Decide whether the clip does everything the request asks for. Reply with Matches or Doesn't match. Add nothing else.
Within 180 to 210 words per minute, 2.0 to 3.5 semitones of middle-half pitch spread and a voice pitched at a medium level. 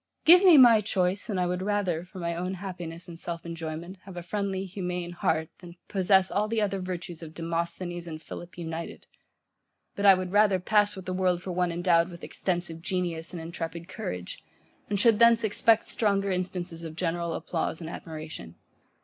Matches